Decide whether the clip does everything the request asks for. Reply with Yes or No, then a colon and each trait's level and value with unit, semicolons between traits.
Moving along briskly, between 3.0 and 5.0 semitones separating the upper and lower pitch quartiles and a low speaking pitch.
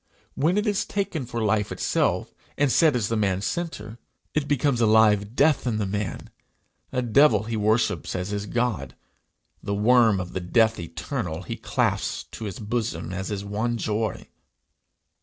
No: average, 170 wpm; average, 3.6 semitones; low, 110 Hz